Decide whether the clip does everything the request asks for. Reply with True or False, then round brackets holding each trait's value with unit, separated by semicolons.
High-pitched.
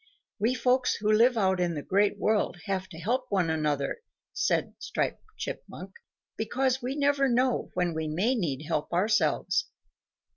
True (205 Hz)